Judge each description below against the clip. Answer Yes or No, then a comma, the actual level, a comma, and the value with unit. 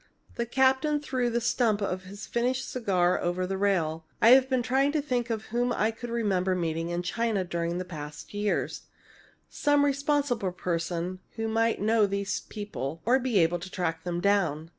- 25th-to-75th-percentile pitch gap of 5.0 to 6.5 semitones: Yes, wide, 5.5 semitones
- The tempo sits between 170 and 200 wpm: Yes, average, 175 wpm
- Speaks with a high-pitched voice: Yes, high, 205 Hz